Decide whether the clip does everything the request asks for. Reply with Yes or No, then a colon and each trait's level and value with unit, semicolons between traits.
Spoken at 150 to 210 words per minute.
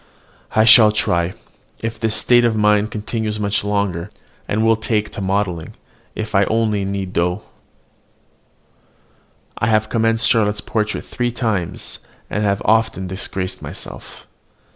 No: average, 140 wpm